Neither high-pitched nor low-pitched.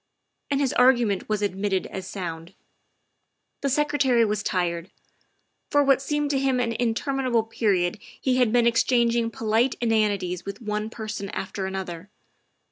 No: high, 225 Hz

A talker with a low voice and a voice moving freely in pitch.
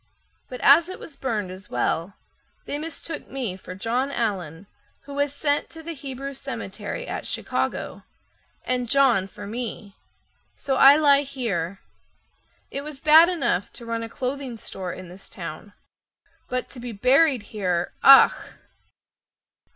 No: very high, 250 Hz; wide, 5.9 semitones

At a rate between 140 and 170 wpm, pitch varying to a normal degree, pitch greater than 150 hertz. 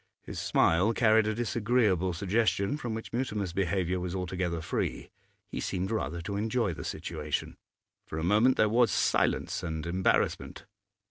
No: average, 150 wpm; average, 3.8 semitones; low, 100 Hz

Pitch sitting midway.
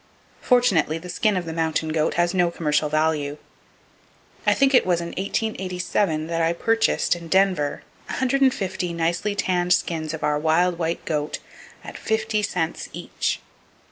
Yes: medium, 175 Hz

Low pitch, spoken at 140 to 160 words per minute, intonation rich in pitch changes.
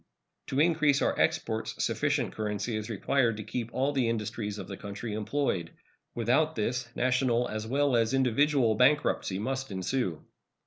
No: low, 120 Hz; average, 150 wpm; average, 4.0 semitones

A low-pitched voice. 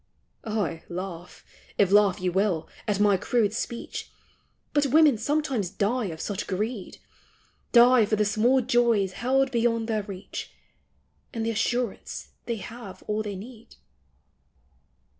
No: high, 215 Hz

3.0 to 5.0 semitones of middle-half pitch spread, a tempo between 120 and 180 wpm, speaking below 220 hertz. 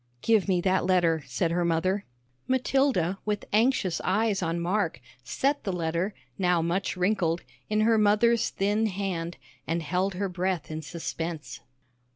Yes: average, 3.7 semitones; average, 150 wpm; medium, 185 Hz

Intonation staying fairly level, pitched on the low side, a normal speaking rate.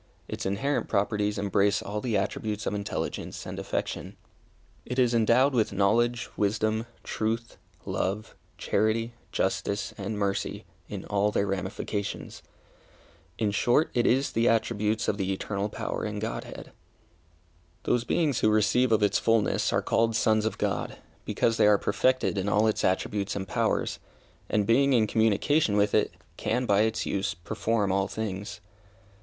Yes: narrow, 2.2 semitones; low, 105 Hz; average, 150 wpm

